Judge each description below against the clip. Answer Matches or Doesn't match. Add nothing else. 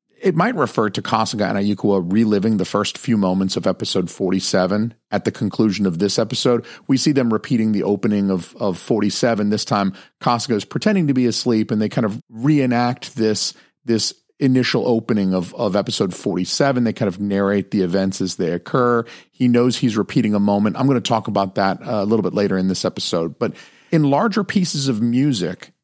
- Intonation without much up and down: Doesn't match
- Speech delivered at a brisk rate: Doesn't match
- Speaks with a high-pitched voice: Doesn't match